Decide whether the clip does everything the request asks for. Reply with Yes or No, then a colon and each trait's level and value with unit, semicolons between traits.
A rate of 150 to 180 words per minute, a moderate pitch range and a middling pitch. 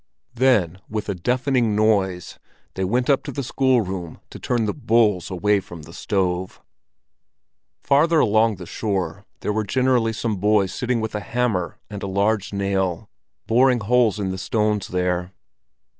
No: average, 160 wpm; average, 3.9 semitones; low, 105 Hz